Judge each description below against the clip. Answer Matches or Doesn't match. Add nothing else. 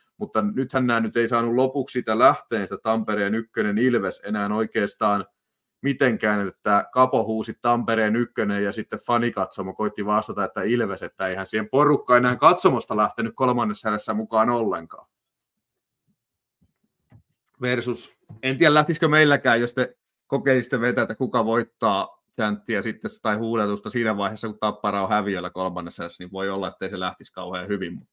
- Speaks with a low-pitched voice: Matches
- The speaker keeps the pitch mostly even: Doesn't match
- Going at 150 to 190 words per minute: Matches